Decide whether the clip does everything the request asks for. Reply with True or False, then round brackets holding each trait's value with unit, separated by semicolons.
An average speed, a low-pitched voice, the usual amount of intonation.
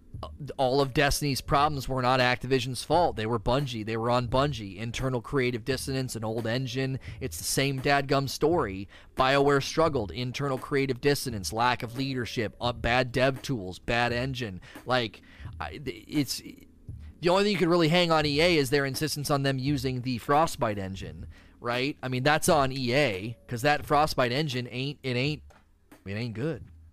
True (175 wpm; 130 Hz; 3.2 semitones)